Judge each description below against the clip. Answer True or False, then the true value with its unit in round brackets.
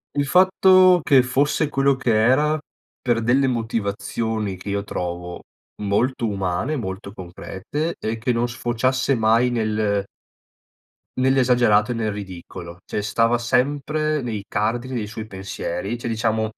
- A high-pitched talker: False (115 Hz)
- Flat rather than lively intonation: False (3.9 semitones)